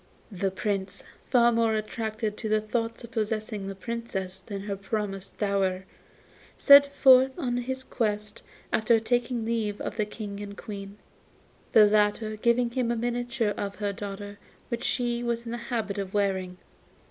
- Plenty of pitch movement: No, average, 2.7 semitones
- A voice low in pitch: No, high, 215 Hz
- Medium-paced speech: Yes, average, 160 wpm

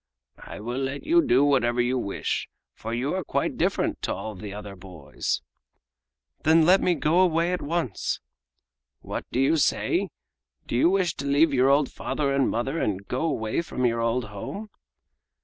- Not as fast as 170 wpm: No, average, 175 wpm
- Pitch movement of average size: No, wide, 5.9 semitones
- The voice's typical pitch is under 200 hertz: Yes, low, 135 Hz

